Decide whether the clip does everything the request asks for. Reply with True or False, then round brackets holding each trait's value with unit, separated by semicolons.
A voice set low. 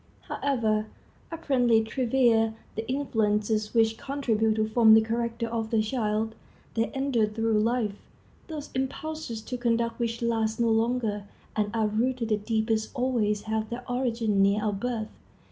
False (225 Hz)